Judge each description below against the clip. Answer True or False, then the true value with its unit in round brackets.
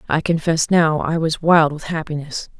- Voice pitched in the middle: True (160 Hz)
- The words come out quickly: False (185 wpm)